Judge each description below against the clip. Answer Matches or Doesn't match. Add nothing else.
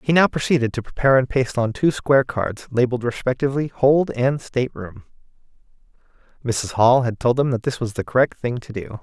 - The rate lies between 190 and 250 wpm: Matches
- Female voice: Doesn't match